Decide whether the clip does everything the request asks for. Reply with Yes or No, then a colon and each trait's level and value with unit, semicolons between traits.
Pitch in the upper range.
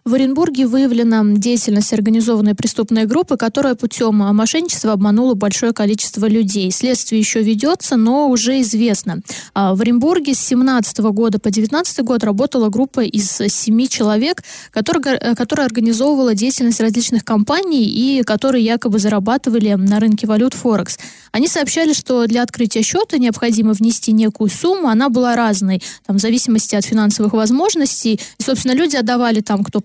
Yes: high, 230 Hz